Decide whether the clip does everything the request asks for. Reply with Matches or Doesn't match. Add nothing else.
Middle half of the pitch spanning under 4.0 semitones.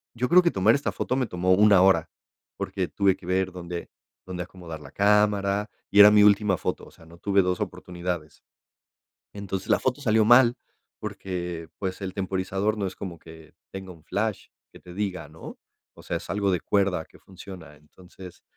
Matches